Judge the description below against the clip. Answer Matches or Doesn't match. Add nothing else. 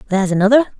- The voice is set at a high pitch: Matches